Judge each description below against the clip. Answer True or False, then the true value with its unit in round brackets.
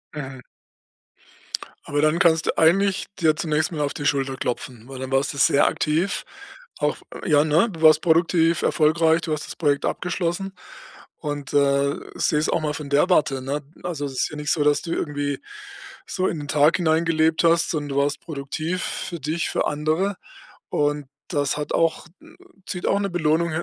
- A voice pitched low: False (155 Hz)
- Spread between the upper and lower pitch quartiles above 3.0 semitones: False (2.6 semitones)